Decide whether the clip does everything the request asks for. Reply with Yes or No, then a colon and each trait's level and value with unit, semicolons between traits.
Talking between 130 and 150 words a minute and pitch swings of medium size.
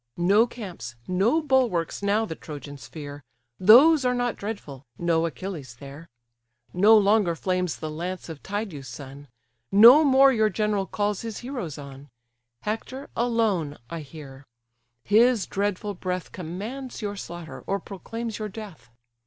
No: average, 140 wpm; wide, 5.9 semitones